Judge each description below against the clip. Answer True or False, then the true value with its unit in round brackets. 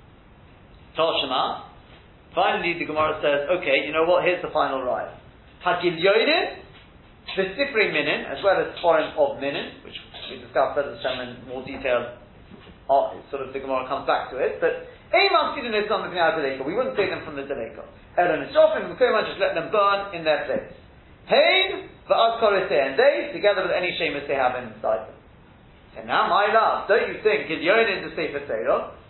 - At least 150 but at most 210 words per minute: True (180 wpm)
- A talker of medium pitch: True (180 Hz)